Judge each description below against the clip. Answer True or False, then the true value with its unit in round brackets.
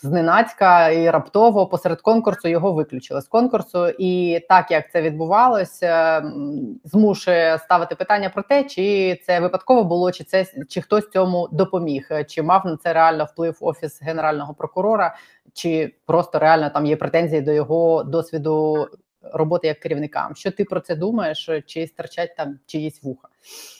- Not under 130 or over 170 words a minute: True (150 wpm)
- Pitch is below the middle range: False (170 Hz)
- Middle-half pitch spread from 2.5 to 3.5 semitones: True (3.2 semitones)